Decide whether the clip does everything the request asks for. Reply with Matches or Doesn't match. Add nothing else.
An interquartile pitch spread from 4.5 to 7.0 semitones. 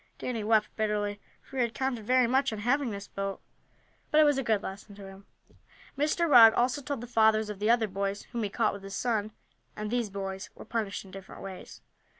Doesn't match